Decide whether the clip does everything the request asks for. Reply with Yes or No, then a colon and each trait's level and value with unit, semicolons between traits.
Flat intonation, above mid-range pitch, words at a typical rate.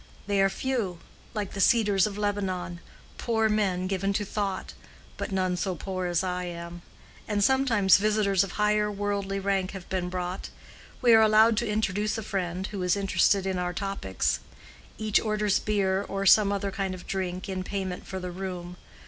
Yes: narrow, 2.2 semitones; high, 195 Hz; average, 175 wpm